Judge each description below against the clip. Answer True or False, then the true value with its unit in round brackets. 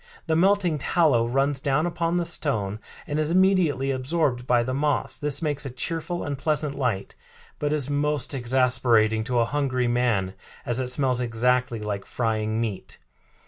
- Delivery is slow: False (165 wpm)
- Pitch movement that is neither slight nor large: True (4.0 semitones)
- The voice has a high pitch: False (130 Hz)